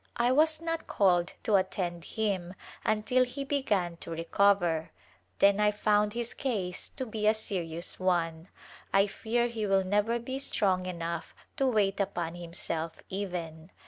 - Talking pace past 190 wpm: No, average, 160 wpm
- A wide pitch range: No, average, 4.2 semitones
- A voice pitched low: No, high, 200 Hz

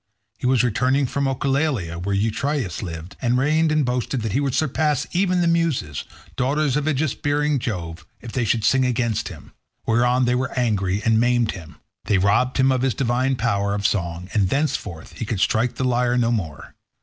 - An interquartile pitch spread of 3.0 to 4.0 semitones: No, average, 4.7 semitones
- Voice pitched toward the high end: No, low, 125 Hz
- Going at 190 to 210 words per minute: Yes, average, 195 wpm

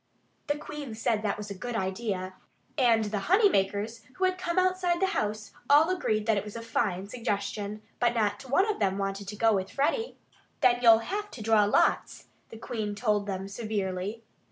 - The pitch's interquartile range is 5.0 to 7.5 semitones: Yes, average, 5.3 semitones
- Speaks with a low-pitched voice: No, high, 220 Hz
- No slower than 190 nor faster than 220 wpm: Yes, average, 200 wpm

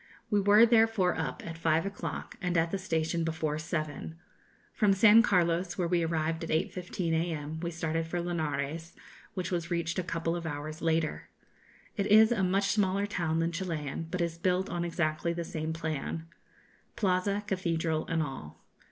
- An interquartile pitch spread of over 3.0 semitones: No, narrow, 2.5 semitones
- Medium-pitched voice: Yes, medium, 170 Hz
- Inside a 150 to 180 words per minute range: Yes, average, 170 wpm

